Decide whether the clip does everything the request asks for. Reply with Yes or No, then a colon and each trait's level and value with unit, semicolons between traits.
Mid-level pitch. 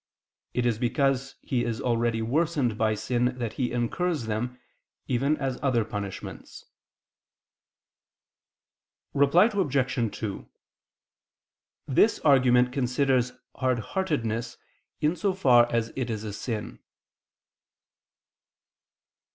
No: low, 125 Hz